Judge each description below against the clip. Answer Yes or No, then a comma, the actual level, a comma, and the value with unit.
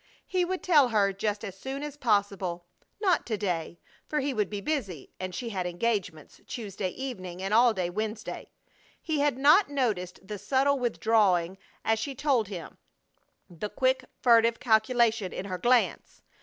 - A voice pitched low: No, high, 220 Hz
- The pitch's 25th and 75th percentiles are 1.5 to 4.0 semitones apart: No, wide, 5.4 semitones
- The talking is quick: No, average, 165 wpm